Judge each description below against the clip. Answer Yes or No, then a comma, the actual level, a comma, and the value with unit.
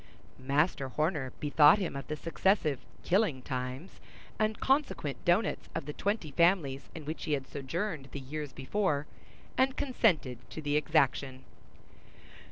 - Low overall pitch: No, medium, 150 Hz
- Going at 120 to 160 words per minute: Yes, average, 140 wpm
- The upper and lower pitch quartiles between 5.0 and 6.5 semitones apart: Yes, average, 5.3 semitones